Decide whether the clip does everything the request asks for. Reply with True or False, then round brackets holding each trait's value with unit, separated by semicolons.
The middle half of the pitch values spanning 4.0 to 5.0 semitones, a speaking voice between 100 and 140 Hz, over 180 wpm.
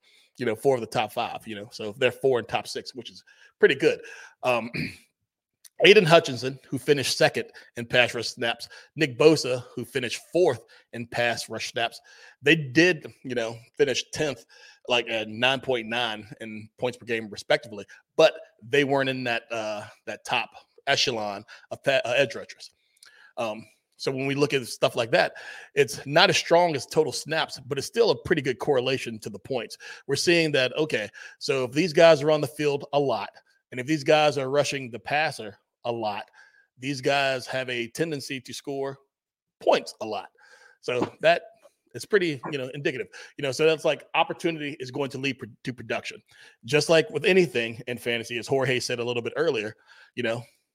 True (4.6 semitones; 135 Hz; 190 wpm)